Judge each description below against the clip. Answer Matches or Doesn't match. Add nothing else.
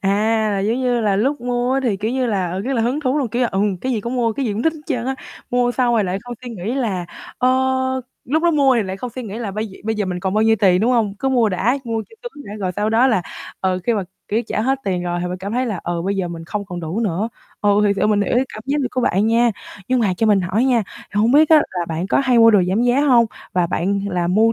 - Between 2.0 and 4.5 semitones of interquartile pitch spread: Matches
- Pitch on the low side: Doesn't match